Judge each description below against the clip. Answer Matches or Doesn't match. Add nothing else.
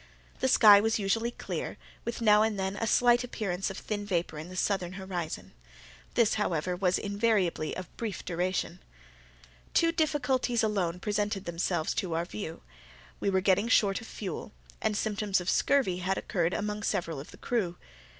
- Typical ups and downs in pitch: Matches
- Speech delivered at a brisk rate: Doesn't match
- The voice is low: Doesn't match